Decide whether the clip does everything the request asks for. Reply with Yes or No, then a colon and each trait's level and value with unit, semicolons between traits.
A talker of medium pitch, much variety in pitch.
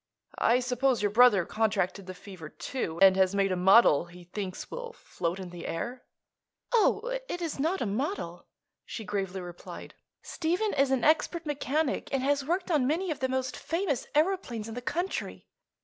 No: very high, 250 Hz; wide, 8.3 semitones